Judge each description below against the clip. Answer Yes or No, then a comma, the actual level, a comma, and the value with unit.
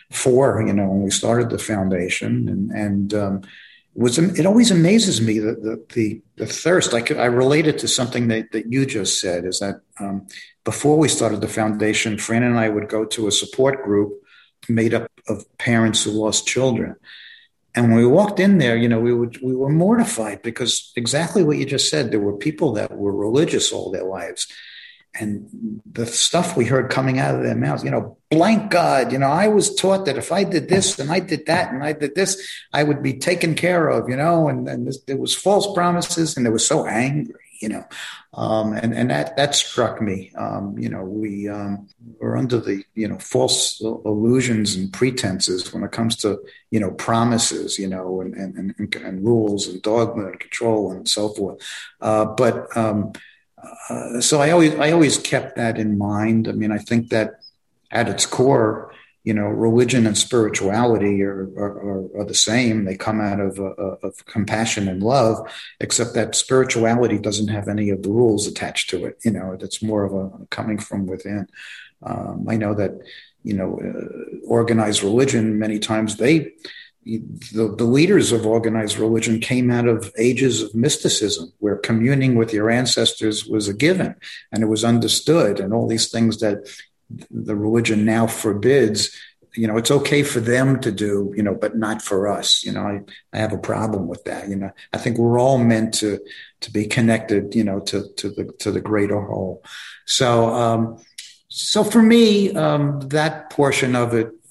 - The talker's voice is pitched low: Yes, low, 115 Hz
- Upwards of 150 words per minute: Yes, average, 195 wpm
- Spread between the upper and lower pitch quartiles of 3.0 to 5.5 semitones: Yes, average, 3.9 semitones